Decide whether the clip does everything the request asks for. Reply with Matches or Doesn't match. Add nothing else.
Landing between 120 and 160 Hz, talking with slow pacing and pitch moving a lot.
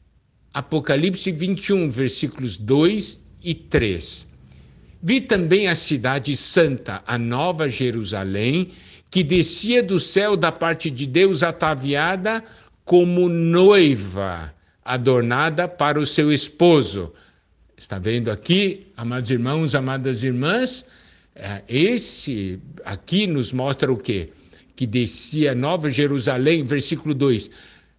Matches